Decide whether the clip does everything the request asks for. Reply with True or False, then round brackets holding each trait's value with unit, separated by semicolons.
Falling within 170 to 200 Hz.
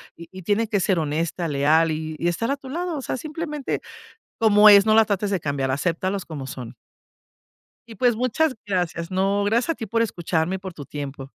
True (190 Hz)